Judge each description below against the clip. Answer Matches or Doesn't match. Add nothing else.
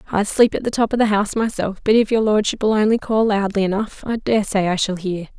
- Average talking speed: Doesn't match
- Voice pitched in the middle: Doesn't match